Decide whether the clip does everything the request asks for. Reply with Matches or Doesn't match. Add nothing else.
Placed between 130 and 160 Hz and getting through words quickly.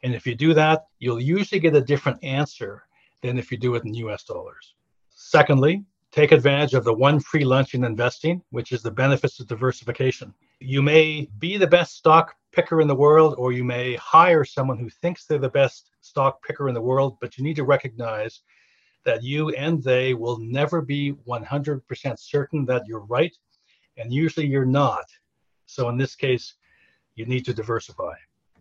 Doesn't match